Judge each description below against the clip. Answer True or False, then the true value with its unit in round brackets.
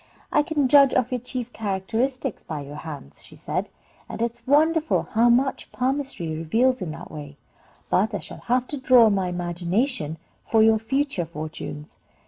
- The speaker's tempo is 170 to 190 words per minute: True (175 wpm)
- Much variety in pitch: True (7.2 semitones)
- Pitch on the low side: False (225 Hz)